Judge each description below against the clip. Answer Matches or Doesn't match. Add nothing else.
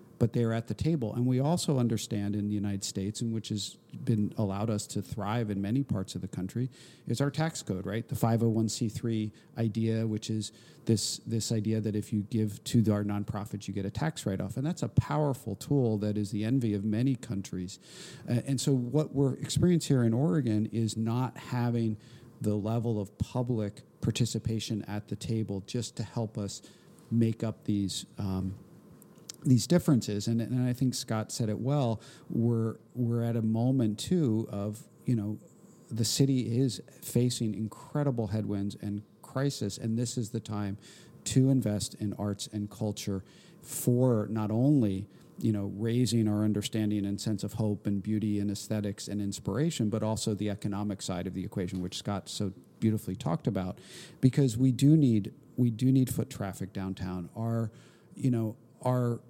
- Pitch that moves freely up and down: Doesn't match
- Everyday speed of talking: Matches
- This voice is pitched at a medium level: Doesn't match